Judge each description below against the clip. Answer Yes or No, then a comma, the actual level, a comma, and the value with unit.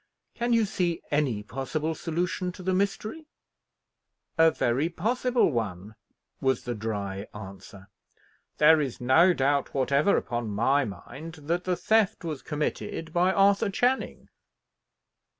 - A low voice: No, medium, 155 Hz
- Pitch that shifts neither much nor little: No, wide, 7.1 semitones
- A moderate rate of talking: No, slow, 130 wpm